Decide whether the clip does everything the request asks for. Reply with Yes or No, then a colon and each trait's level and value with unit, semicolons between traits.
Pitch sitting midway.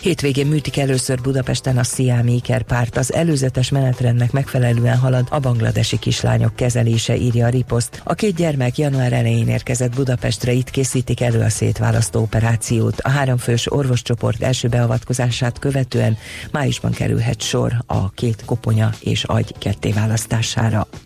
No: low, 125 Hz